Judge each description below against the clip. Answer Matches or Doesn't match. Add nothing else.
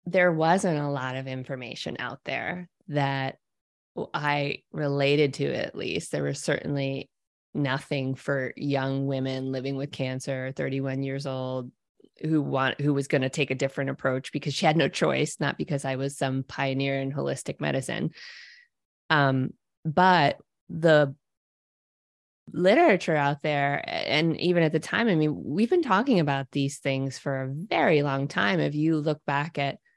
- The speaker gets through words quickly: Doesn't match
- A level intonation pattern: Matches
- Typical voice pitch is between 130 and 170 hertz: Matches